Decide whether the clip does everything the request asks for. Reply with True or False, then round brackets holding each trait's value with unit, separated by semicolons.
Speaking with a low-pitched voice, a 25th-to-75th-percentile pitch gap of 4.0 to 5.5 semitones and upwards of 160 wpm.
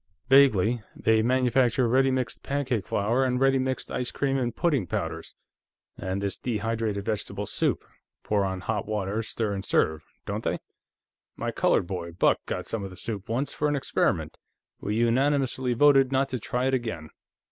True (115 Hz; 4.5 semitones; 170 wpm)